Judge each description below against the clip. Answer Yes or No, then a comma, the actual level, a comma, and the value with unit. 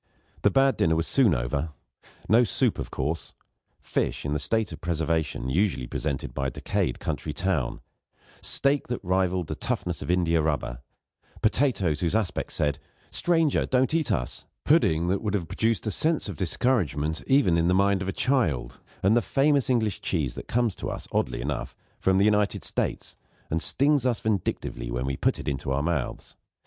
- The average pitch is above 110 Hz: No, very low, 90 Hz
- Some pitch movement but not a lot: No, wide, 7.1 semitones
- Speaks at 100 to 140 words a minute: No, average, 180 wpm